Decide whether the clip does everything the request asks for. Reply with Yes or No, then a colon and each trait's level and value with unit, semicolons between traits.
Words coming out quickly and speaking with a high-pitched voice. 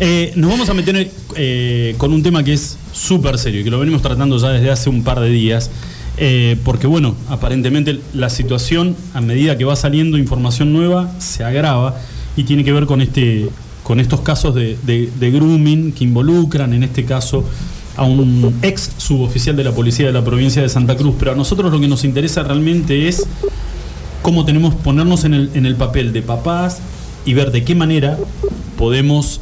No: fast, 195 wpm; medium, 140 Hz